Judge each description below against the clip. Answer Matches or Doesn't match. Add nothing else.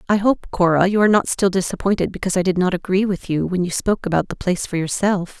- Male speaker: Doesn't match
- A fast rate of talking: Matches